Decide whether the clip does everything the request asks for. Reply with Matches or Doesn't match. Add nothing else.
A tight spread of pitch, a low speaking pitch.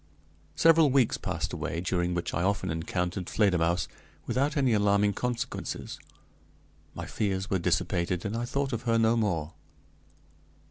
Doesn't match